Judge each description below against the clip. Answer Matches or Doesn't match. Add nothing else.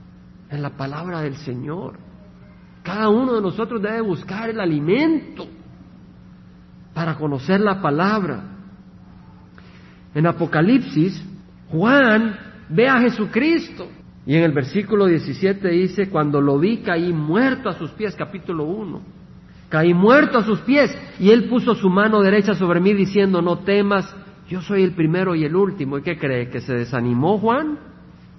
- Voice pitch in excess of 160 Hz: Matches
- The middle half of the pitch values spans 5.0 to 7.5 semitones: Matches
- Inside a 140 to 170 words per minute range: Matches